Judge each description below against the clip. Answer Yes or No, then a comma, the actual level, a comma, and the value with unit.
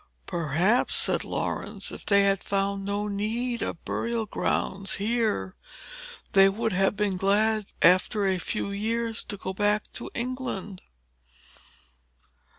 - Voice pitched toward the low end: No, high, 200 Hz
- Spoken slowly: Yes, slow, 130 wpm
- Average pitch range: No, narrow, 2.3 semitones